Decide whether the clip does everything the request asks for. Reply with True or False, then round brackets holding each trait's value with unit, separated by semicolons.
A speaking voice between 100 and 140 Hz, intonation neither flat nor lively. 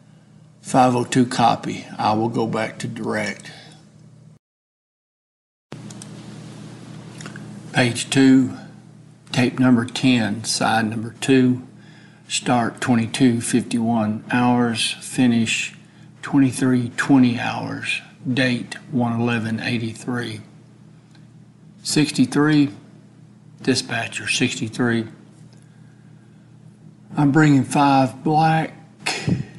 True (135 Hz; 4.7 semitones)